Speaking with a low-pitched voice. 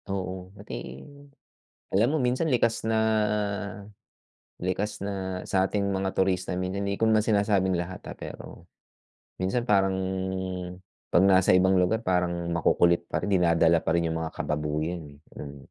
Yes: very low, 95 Hz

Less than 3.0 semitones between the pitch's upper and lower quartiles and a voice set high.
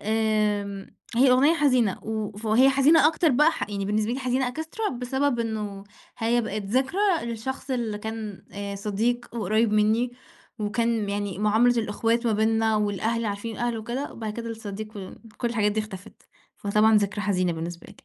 Yes: narrow, 2.6 semitones; high, 220 Hz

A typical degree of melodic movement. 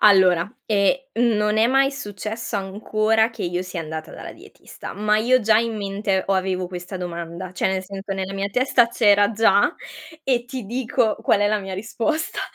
Yes: average, 3.1 semitones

